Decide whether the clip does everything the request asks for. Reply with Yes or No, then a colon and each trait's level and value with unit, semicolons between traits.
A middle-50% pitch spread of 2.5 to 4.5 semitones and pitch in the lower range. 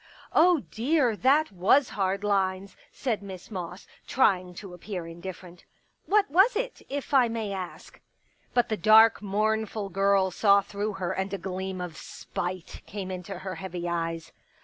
No: average, 3.3 semitones; high, 195 Hz